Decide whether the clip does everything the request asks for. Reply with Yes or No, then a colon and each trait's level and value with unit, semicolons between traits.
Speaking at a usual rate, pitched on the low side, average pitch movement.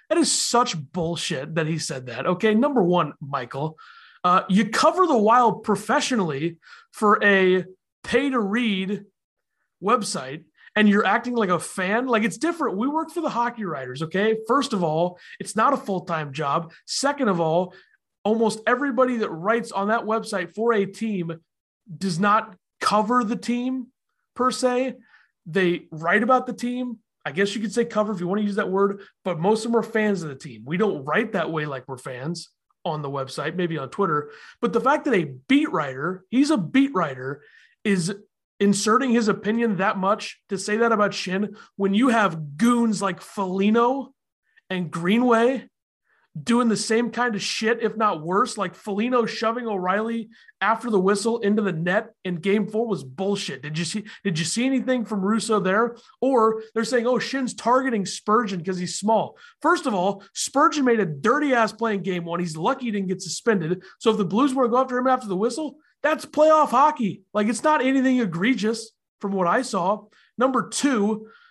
No: average, 190 wpm; high, 215 Hz; average, 4.3 semitones